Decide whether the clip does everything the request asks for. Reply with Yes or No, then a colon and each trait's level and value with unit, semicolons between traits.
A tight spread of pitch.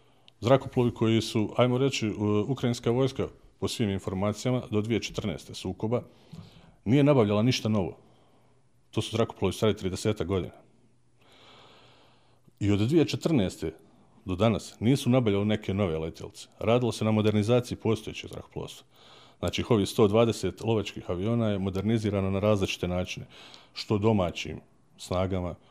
No: average, 3.3 semitones